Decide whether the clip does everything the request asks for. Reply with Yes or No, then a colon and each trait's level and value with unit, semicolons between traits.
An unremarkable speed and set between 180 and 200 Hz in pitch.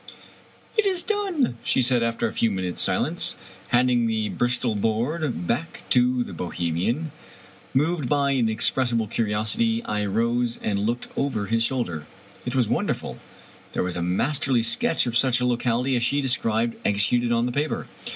No: average, 170 wpm; low, 120 Hz